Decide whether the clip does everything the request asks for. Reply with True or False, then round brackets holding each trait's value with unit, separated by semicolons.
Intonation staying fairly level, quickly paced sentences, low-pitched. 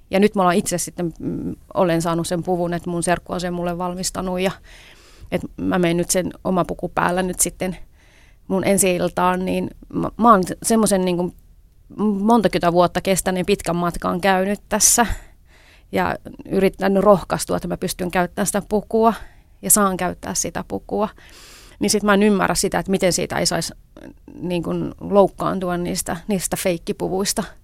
False (2.0 semitones; 160 wpm; 185 Hz)